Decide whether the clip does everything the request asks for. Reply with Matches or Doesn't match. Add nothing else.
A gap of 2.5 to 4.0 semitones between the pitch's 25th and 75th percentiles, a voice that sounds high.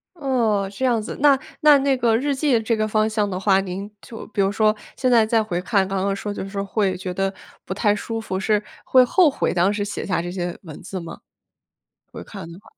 Matches